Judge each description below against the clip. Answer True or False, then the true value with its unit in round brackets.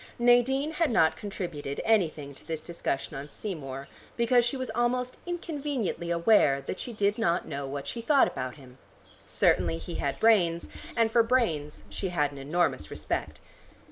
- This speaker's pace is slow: False (165 wpm)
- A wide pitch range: True (8.9 semitones)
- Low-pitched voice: False (175 Hz)